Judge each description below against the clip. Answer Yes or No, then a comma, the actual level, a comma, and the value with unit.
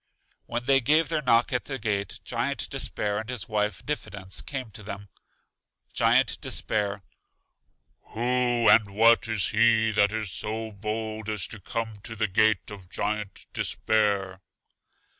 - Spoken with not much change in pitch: Yes, narrow, 2.3 semitones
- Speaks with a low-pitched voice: Yes, low, 110 Hz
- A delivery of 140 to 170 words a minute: Yes, average, 145 wpm